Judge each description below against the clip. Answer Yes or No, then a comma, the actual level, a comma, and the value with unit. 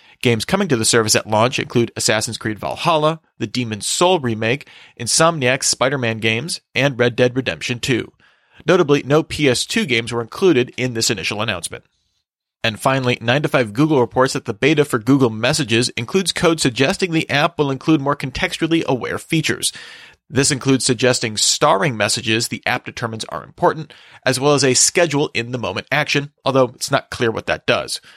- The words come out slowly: No, average, 180 wpm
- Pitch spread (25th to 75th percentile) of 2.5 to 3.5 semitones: No, average, 4.1 semitones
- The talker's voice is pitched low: Yes, low, 125 Hz